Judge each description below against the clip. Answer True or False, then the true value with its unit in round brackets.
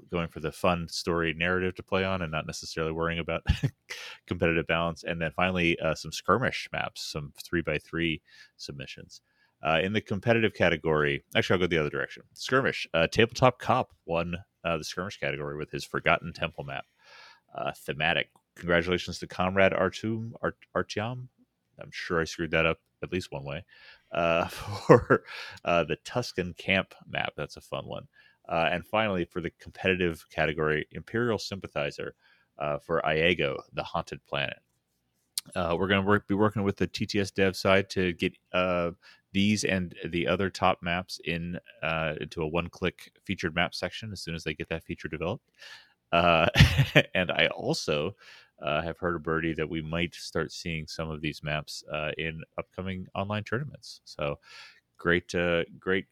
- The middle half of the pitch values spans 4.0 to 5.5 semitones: False (2.9 semitones)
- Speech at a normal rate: True (170 wpm)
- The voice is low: True (85 Hz)